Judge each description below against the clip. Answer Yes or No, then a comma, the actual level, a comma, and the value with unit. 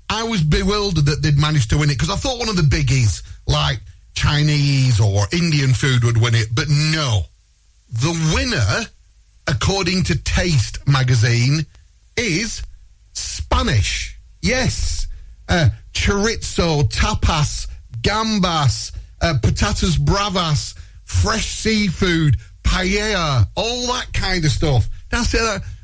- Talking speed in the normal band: No, slow, 120 wpm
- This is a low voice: Yes, low, 125 Hz